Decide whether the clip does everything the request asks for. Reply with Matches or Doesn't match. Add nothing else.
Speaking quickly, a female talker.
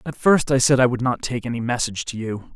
Doesn't match